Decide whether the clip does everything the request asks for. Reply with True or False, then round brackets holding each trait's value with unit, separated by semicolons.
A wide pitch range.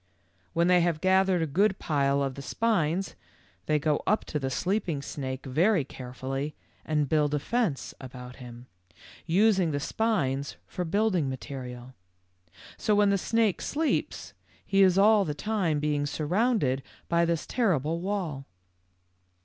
True (6.0 semitones)